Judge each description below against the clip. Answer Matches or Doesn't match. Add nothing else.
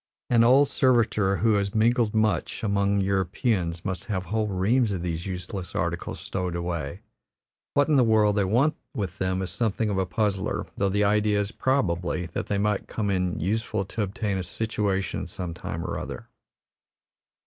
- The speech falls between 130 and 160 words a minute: Doesn't match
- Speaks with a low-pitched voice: Matches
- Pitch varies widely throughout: Doesn't match